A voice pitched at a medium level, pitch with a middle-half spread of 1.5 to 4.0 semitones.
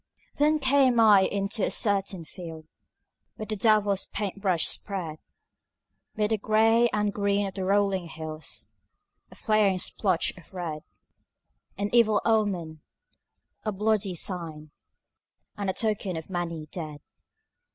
No: high, 200 Hz; average, 3.5 semitones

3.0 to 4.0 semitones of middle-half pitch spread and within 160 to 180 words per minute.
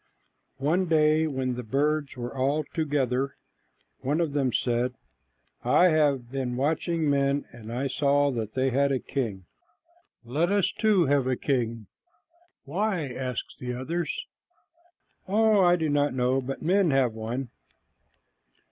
No: average, 3.7 semitones; average, 140 wpm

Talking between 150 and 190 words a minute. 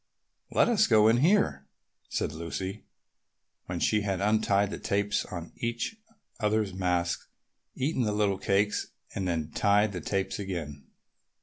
No: average, 140 wpm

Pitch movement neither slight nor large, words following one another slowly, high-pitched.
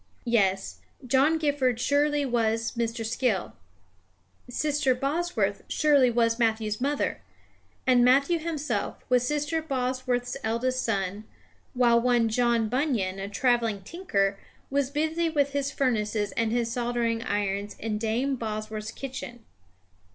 Yes: average, 3.9 semitones; slow, 120 wpm; high, 245 Hz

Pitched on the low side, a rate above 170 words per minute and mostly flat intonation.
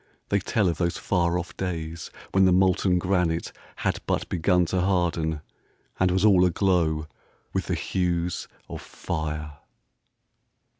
No: very low, 90 Hz; average, 140 wpm; narrow, 2.2 semitones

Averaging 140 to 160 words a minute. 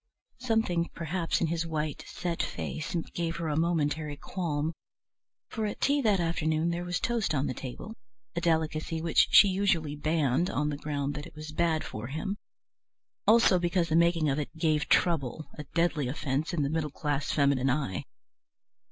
No: average, 175 wpm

